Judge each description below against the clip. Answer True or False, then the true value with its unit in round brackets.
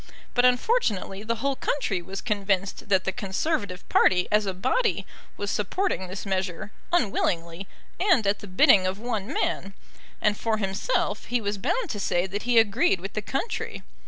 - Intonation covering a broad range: False (4.0 semitones)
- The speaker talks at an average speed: True (170 wpm)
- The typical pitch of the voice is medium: False (205 Hz)